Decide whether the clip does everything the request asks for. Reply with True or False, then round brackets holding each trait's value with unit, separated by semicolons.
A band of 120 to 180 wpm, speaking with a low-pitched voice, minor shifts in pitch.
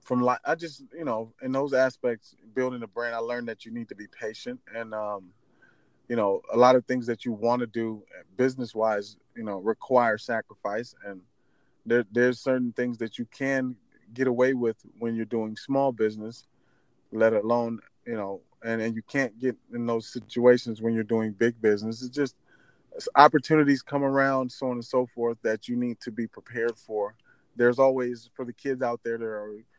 False (195 wpm; 120 Hz; 2.2 semitones)